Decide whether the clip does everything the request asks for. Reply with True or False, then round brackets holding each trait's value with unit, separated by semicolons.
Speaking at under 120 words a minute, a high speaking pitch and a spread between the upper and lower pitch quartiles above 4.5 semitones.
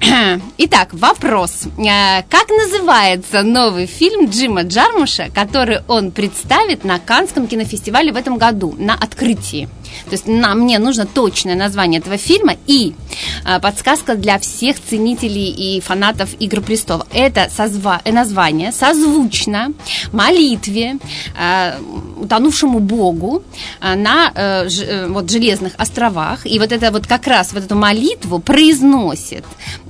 True (110 wpm; 220 Hz; 5.2 semitones)